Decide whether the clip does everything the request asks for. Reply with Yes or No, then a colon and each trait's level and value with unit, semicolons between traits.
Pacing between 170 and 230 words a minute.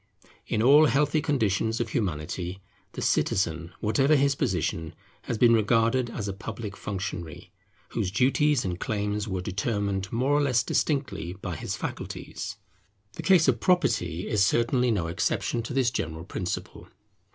No: average, 150 wpm